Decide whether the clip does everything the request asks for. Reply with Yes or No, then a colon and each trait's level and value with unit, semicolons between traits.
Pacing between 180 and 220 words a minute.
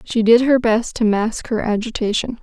Yes: average, 200 wpm